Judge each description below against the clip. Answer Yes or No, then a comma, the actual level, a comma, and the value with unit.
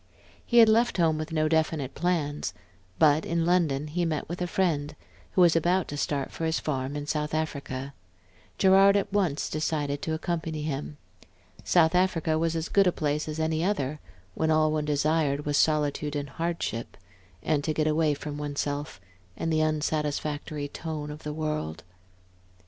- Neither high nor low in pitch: Yes, medium, 155 Hz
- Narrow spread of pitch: Yes, narrow, 2.0 semitones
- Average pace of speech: Yes, average, 170 wpm